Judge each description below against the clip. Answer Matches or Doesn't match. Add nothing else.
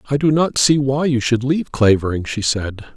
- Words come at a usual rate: Doesn't match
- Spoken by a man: Matches